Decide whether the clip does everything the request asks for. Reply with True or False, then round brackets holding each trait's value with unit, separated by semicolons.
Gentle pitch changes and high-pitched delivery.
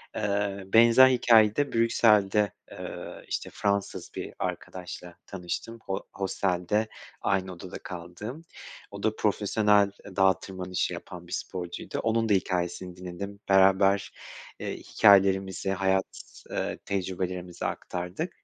False (2.3 semitones; 95 Hz)